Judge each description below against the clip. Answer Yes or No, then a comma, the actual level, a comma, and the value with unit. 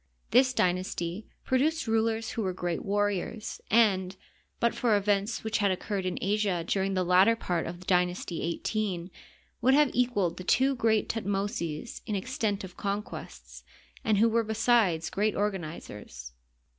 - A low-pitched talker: No, high, 205 Hz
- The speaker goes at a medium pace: Yes, average, 150 wpm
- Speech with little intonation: No, average, 3.6 semitones